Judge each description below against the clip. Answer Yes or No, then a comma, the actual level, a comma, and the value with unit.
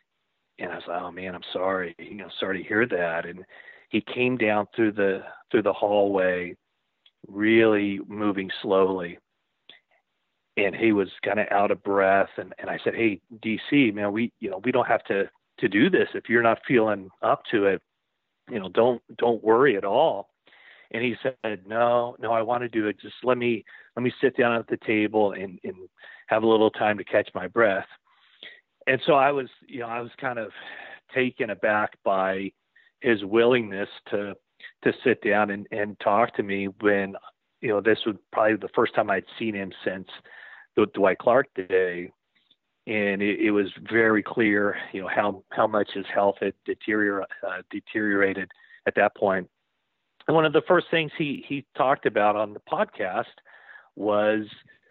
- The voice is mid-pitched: No, low, 105 Hz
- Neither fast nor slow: Yes, average, 185 wpm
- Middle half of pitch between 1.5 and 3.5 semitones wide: Yes, average, 2.9 semitones